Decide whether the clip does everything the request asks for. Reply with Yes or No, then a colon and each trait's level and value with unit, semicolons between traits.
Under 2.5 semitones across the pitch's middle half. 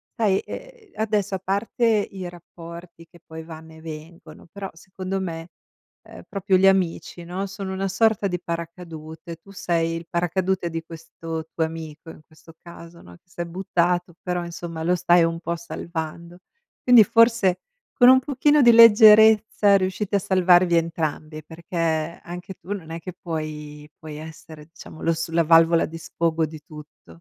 No: average, 2.8 semitones